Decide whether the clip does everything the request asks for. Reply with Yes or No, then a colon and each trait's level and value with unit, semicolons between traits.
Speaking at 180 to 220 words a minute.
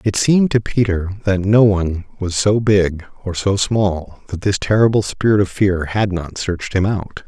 Yes: average, 200 wpm